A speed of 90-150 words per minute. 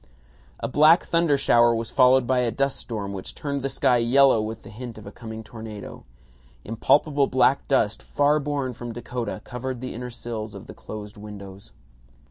No: average, 180 wpm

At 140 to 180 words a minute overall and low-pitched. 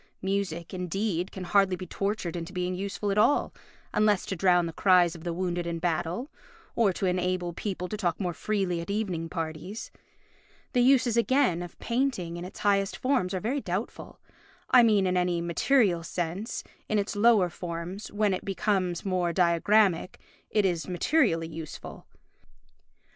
No: average, 160 wpm; medium, 185 Hz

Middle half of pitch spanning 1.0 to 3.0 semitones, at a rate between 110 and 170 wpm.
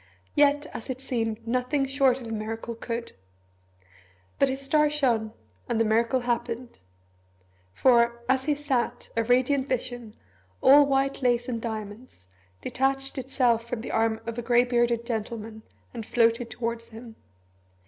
Yes: narrow, 2.5 semitones; average, 150 wpm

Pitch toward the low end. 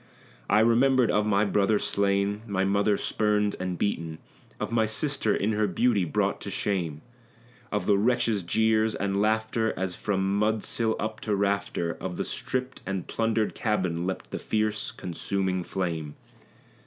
Yes: low, 105 Hz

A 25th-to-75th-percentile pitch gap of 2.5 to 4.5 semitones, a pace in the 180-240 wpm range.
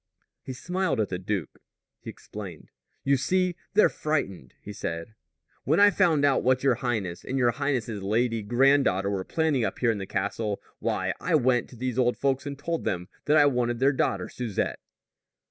No: average, 5.3 semitones; average, 185 wpm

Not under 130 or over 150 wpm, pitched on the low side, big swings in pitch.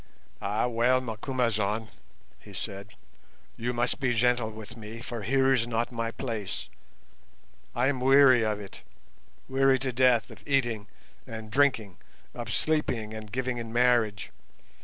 No: average, 140 wpm; low, 120 Hz; average, 2.7 semitones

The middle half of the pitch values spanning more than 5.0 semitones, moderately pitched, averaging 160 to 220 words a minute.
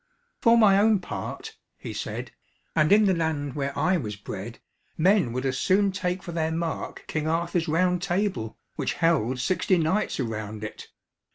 Yes: wide, 5.4 semitones; medium, 165 Hz; average, 170 wpm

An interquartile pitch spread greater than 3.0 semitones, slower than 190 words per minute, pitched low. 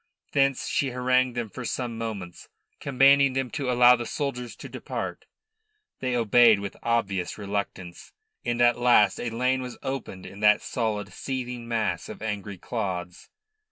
Yes: average, 3.6 semitones; average, 155 wpm; low, 120 Hz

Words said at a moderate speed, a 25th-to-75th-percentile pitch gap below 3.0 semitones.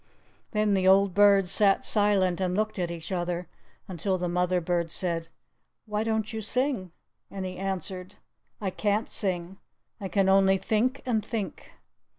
Yes: average, 160 wpm; narrow, 2.6 semitones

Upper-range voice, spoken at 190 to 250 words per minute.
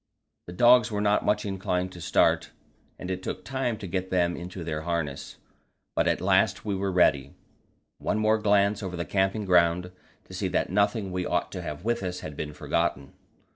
No: very low, 95 Hz; average, 195 wpm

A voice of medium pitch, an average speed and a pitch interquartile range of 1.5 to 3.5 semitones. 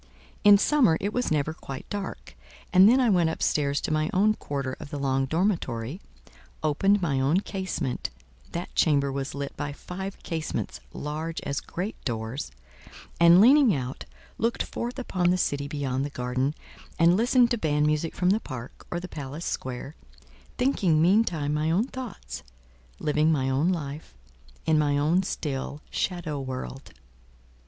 No: medium, 155 Hz; average, 160 wpm; average, 5.2 semitones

